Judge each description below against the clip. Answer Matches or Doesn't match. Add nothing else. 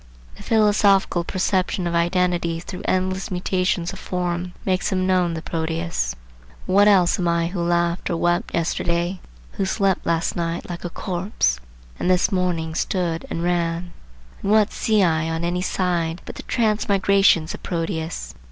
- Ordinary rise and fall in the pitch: Doesn't match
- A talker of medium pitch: Matches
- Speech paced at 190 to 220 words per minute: Doesn't match